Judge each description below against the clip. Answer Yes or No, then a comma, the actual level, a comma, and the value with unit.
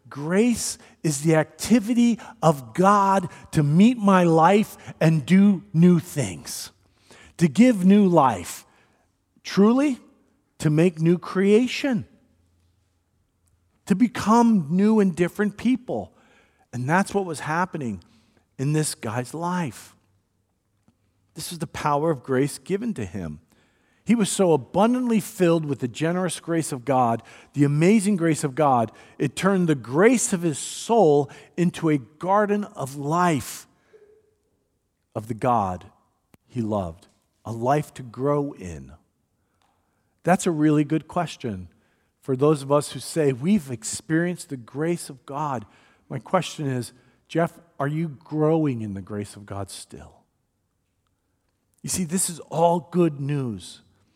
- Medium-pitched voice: Yes, medium, 150 Hz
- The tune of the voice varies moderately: No, wide, 8.0 semitones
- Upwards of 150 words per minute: No, slow, 135 wpm